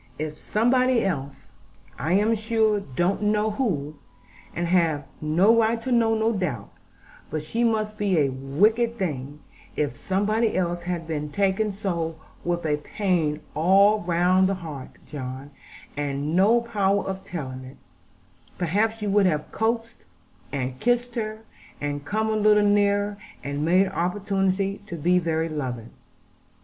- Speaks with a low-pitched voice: No, high, 190 Hz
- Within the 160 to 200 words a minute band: No, average, 150 wpm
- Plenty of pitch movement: Yes, wide, 5.7 semitones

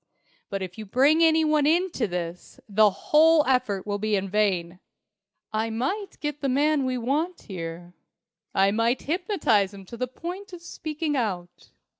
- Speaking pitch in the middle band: No, high, 245 Hz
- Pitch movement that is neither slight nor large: No, wide, 7.6 semitones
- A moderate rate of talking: Yes, average, 160 wpm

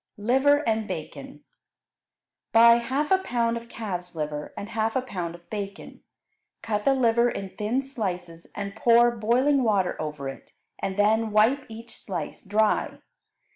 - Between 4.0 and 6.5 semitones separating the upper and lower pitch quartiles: No, average, 3.5 semitones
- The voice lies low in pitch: No, high, 220 Hz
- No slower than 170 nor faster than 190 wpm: No, average, 150 wpm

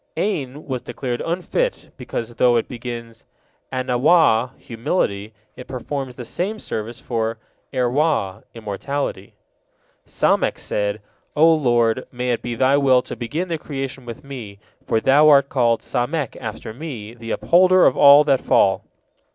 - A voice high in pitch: No, low, 125 Hz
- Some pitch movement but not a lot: Yes, average, 3.9 semitones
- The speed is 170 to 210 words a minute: No, average, 145 wpm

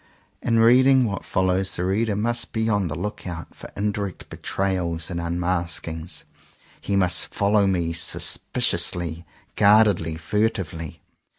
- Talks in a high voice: No, very low, 95 Hz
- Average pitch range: Yes, average, 3.6 semitones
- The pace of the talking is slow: Yes, slow, 125 wpm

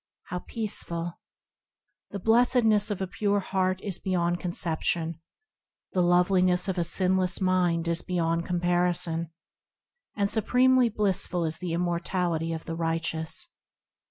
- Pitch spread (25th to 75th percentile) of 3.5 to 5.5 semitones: No, narrow, 2.5 semitones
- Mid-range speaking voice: Yes, medium, 180 Hz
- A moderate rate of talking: No, slow, 125 wpm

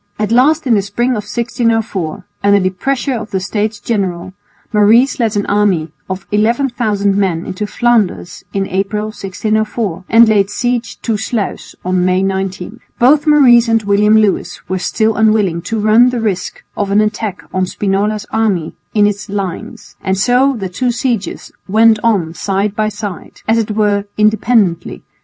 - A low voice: No, high, 210 Hz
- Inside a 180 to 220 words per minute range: No, average, 165 wpm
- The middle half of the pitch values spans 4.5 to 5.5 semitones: No, average, 2.8 semitones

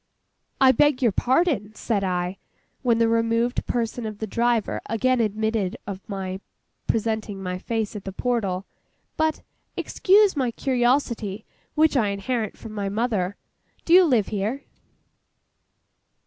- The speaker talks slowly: Yes, slow, 130 wpm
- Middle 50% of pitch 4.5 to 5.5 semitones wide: No, average, 3.8 semitones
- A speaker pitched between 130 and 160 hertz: No, high, 225 Hz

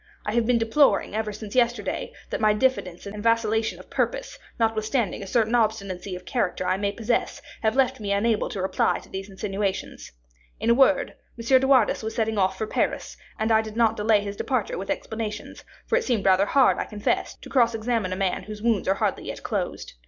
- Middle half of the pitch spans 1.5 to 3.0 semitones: Yes, average, 2.7 semitones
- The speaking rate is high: Yes, fast, 210 wpm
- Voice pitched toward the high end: Yes, high, 220 Hz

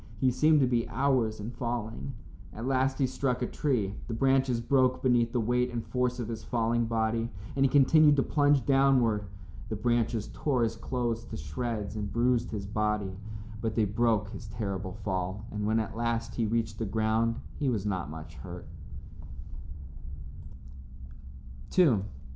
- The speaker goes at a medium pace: Yes, average, 165 wpm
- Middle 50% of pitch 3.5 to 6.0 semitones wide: No, average, 2.9 semitones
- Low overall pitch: Yes, low, 115 Hz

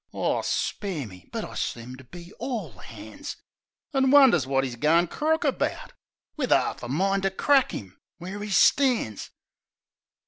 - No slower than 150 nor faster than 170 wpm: Yes, average, 160 wpm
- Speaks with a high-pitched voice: No, medium, 175 Hz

